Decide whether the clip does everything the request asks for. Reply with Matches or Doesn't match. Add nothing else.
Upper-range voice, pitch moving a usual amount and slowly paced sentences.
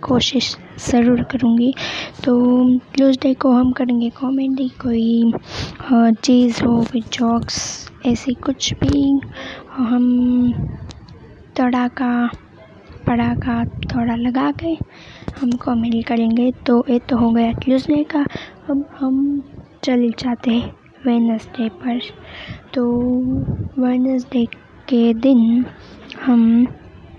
Doesn't match